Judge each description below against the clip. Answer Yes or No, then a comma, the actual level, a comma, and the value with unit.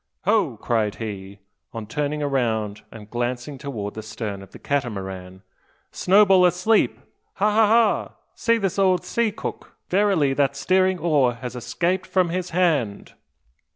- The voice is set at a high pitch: No, medium, 140 Hz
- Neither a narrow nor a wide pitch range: No, wide, 8.8 semitones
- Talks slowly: No, average, 145 wpm